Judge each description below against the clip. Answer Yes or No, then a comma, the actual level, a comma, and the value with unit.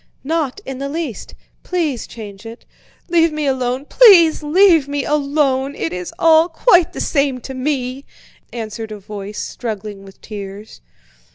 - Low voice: No, very high, 270 Hz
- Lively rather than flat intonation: Yes, wide, 6.1 semitones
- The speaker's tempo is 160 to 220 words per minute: No, average, 150 wpm